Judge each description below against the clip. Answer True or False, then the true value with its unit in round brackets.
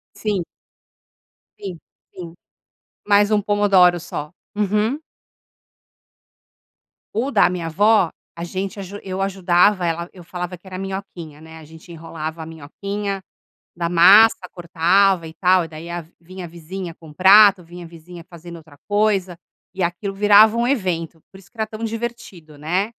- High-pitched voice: False (180 Hz)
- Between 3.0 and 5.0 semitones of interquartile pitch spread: True (3.3 semitones)